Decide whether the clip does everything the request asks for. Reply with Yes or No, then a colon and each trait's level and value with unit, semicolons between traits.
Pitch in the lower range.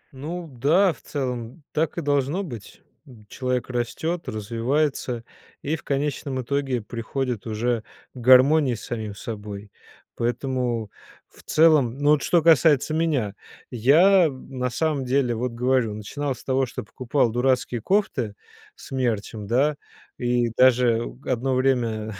Yes: low, 130 Hz